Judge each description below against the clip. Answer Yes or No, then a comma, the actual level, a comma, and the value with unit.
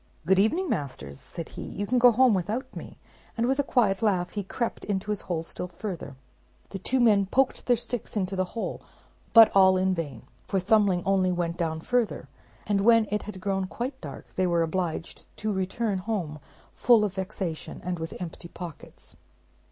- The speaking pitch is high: Yes, high, 195 Hz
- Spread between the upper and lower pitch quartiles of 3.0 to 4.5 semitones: Yes, average, 3.9 semitones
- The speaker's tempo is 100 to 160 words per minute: No, average, 190 wpm